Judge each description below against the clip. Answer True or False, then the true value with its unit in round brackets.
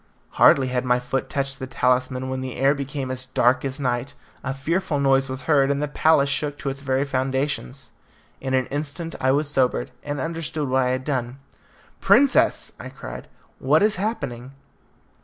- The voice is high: False (135 Hz)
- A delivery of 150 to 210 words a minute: True (180 wpm)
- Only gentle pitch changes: True (1.9 semitones)